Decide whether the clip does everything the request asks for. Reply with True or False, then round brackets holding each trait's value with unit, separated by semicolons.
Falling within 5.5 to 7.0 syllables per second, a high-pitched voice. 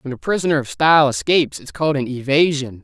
False (6.5 syllables/s; 145 Hz)